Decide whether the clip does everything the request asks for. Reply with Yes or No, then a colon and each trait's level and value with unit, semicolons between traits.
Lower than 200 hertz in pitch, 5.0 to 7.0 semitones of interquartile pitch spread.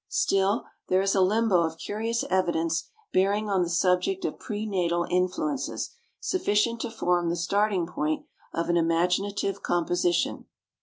No: medium, 185 Hz; average, 3.3 semitones